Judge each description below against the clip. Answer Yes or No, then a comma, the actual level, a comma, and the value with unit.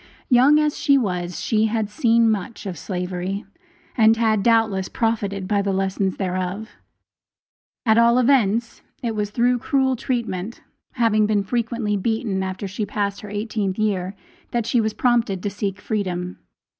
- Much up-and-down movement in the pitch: No, average, 3.1 semitones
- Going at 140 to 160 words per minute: Yes, average, 155 wpm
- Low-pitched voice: No, high, 215 Hz